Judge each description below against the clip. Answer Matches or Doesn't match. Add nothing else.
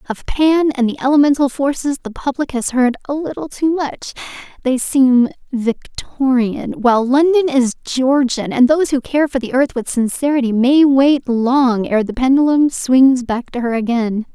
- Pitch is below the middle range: Doesn't match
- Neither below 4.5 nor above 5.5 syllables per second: Matches